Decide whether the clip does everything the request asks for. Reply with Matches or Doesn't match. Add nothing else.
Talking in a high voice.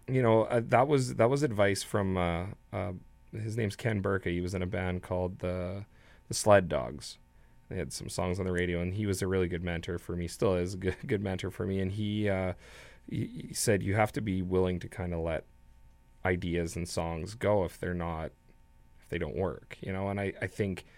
Doesn't match